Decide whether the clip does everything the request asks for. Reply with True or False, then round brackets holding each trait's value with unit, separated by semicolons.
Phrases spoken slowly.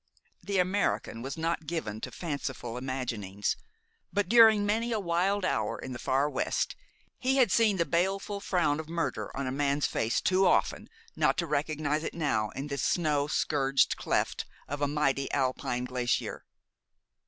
False (165 wpm)